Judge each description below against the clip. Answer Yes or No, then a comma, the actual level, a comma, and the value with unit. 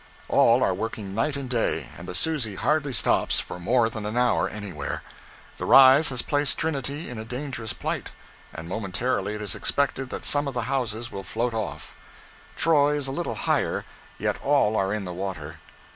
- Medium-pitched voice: No, low, 120 Hz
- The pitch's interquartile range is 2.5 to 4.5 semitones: No, average, 5.0 semitones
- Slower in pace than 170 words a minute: No, average, 190 wpm